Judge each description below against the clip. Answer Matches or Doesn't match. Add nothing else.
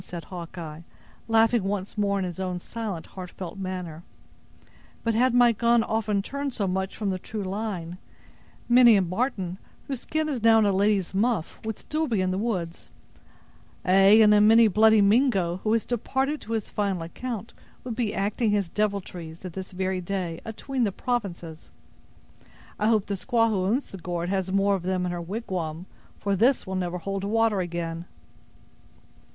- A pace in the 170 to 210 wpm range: Matches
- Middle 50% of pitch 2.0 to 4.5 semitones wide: Matches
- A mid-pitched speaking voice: Doesn't match